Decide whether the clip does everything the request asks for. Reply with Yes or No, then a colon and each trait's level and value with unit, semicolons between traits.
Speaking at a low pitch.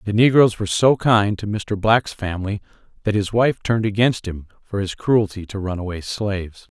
Yes: low, 105 Hz